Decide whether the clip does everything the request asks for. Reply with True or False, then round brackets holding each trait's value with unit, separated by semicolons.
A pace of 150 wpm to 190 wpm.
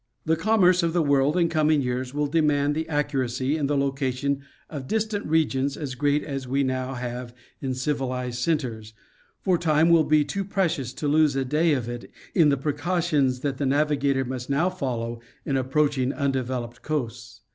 True (180 wpm)